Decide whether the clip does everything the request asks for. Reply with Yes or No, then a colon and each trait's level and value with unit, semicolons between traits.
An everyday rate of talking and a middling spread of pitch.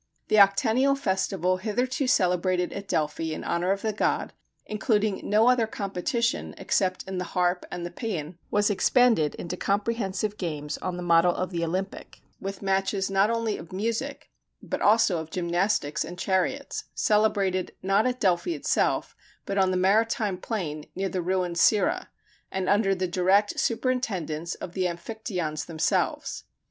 Yes: average, 155 wpm; average, 3.3 semitones